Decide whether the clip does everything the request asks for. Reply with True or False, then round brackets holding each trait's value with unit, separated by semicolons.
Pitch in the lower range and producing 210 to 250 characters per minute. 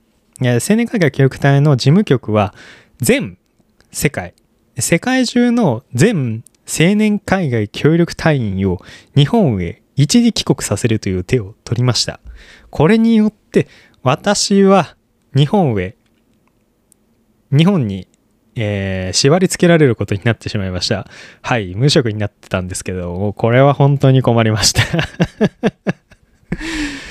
True (125 Hz; 240 characters per minute)